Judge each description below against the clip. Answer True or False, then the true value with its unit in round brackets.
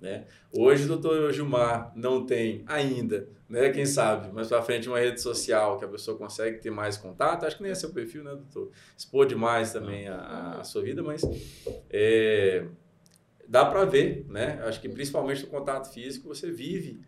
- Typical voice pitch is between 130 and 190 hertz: True (140 Hz)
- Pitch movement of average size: False (8.8 semitones)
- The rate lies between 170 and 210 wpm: True (185 wpm)